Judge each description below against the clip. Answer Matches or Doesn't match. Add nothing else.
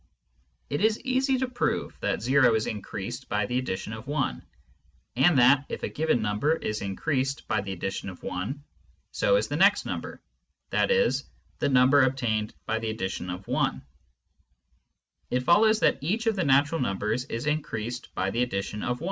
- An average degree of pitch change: Doesn't match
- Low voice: Matches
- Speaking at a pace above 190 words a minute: Doesn't match